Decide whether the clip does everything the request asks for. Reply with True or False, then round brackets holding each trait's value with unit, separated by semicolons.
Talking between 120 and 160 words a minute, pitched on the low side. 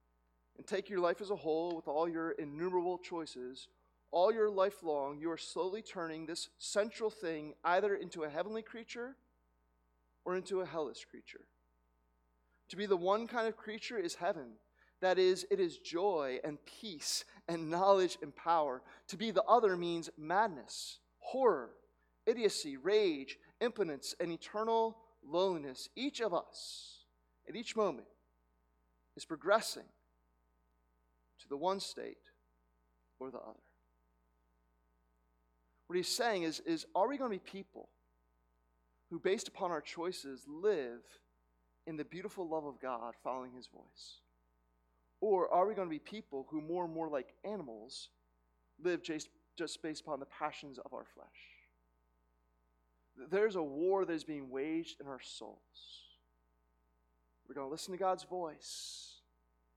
False (150 wpm; 150 Hz)